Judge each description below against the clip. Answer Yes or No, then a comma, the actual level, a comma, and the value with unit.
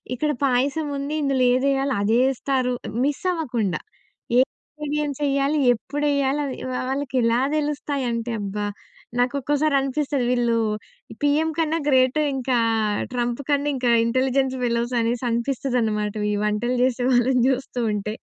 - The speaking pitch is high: Yes, very high, 260 Hz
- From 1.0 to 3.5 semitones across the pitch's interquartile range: Yes, average, 2.9 semitones